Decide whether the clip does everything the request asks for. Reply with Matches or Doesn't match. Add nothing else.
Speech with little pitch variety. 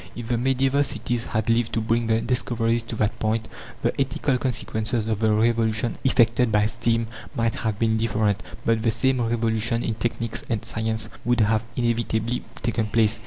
Matches